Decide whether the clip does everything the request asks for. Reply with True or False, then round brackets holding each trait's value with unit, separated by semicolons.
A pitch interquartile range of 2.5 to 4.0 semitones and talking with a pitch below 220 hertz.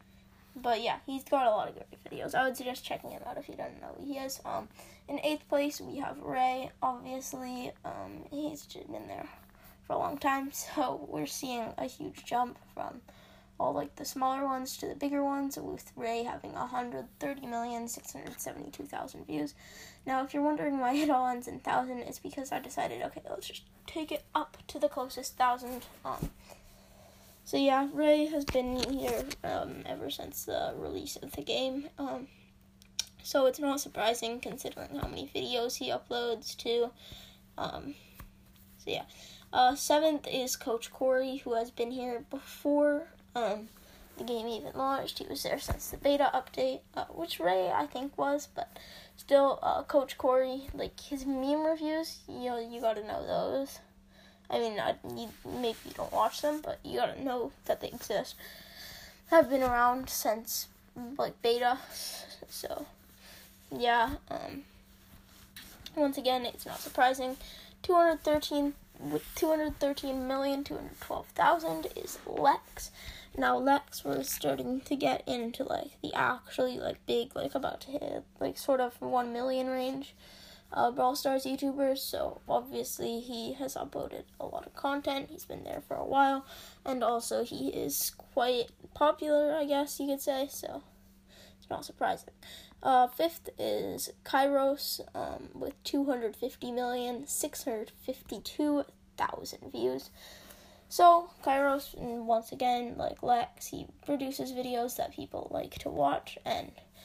False (3.2 semitones; 270 Hz)